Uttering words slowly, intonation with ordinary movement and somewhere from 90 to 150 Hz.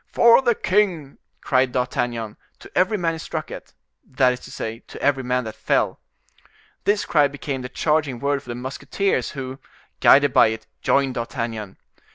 No: average, 175 wpm; average, 4.1 semitones; low, 135 Hz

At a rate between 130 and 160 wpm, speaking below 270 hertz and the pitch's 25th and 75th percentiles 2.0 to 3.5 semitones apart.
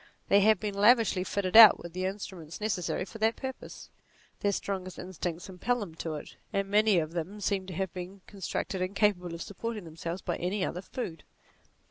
No: average, 185 wpm; high, 190 Hz; average, 2.8 semitones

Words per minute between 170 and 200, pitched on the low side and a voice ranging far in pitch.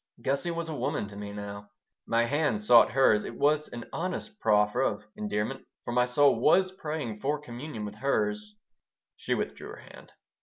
Yes: average, 180 wpm; low, 130 Hz; wide, 6.4 semitones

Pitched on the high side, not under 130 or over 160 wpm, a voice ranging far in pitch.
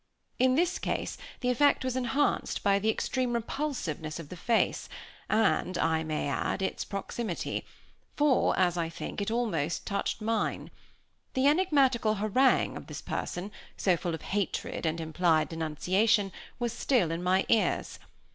Yes: high, 205 Hz; average, 150 wpm; wide, 6.5 semitones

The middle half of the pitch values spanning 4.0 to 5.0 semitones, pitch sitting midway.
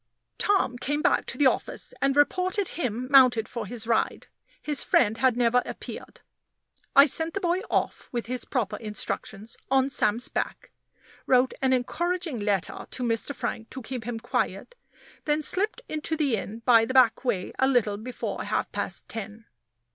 No: average, 4.3 semitones; very high, 255 Hz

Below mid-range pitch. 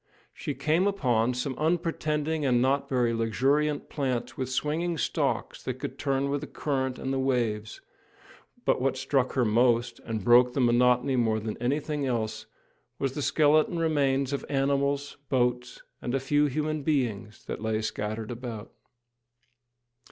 Yes: low, 130 Hz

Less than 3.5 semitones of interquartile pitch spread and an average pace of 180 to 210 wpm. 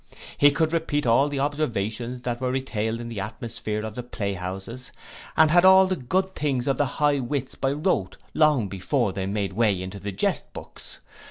No: wide, 5.6 semitones; average, 190 wpm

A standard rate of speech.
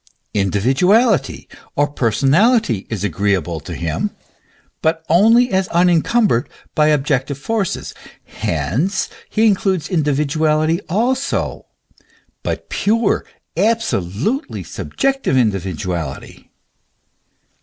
No: slow, 85 wpm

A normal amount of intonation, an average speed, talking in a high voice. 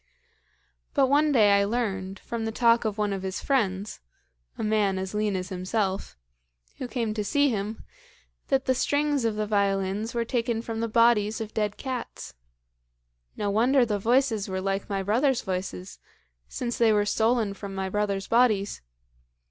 Yes: average, 3.2 semitones; average, 170 wpm; high, 215 Hz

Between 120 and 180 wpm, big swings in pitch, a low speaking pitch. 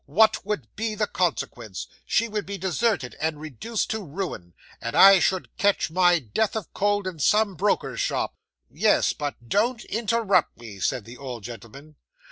No: average, 170 wpm; wide, 7.7 semitones; medium, 185 Hz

